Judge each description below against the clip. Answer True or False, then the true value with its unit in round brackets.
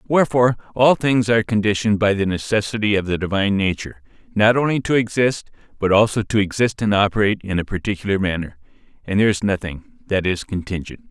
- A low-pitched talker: True (105 Hz)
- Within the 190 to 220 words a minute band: False (180 wpm)